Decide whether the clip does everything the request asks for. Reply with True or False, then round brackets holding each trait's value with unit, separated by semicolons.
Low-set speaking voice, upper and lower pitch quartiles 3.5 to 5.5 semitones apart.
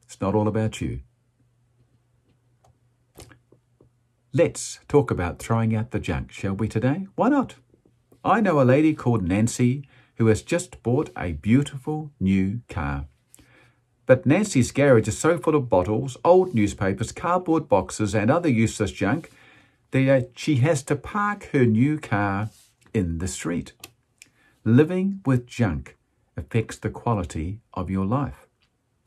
True (120 Hz; 4.4 semitones)